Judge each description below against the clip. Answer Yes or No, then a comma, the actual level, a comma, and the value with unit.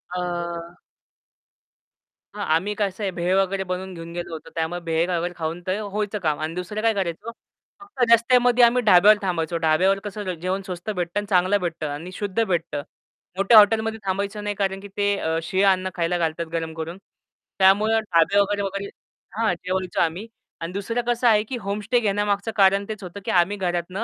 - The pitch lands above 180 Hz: Yes, high, 190 Hz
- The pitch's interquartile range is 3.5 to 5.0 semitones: No, average, 3.1 semitones